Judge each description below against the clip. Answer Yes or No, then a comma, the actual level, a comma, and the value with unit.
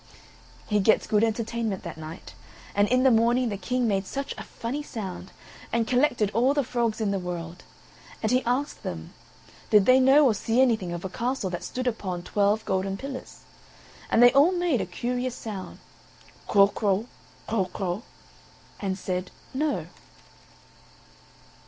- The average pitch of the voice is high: Yes, high, 220 Hz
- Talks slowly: No, average, 160 wpm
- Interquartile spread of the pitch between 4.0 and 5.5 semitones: Yes, average, 4.6 semitones